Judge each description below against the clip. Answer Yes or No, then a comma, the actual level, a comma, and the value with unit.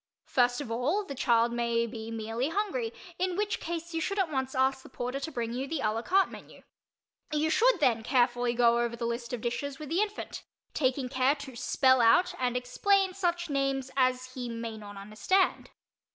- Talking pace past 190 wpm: Yes, average, 200 wpm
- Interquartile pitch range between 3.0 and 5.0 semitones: No, wide, 5.4 semitones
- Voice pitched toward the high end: Yes, very high, 260 Hz